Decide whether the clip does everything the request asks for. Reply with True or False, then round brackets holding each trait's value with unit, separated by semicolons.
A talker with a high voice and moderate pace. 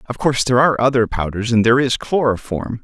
False (120 Hz; 190 wpm)